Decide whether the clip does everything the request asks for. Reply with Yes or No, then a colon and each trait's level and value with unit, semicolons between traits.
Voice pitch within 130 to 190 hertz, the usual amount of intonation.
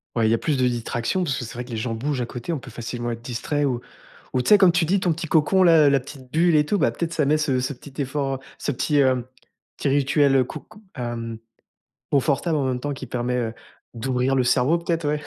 Yes: low, 135 Hz; average, 3.7 semitones